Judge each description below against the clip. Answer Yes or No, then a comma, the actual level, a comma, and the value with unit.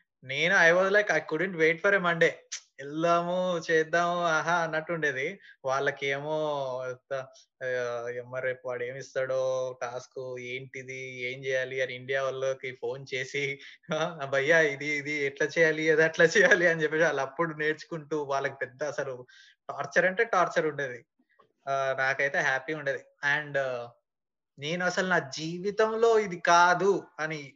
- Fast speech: Yes, fast, 135 wpm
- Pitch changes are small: No, average, 4.2 semitones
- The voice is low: No, medium, 145 Hz